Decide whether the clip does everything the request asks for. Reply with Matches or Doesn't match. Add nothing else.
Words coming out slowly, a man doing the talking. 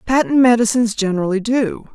Doesn't match